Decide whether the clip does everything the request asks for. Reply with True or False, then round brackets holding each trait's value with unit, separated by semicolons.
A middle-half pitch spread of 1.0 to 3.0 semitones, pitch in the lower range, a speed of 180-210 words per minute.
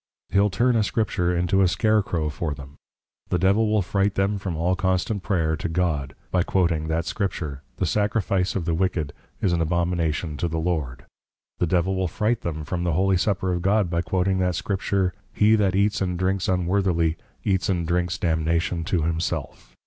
True (2.6 semitones; 90 Hz; 190 wpm)